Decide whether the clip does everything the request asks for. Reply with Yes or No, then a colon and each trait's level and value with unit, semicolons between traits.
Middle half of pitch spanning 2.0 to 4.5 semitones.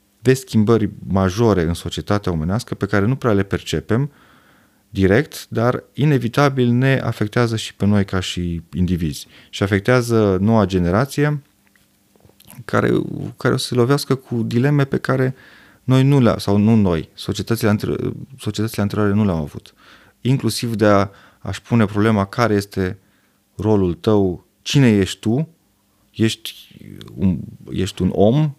Yes: average, 3.9 semitones